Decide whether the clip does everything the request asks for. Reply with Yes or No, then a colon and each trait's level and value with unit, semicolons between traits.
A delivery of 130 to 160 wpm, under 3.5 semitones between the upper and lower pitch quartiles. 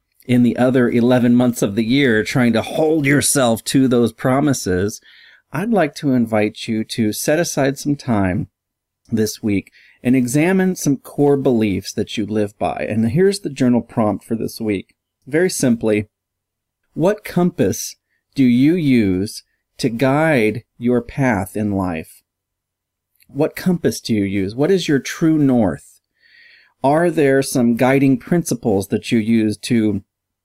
No: average, 150 wpm; average, 5.3 semitones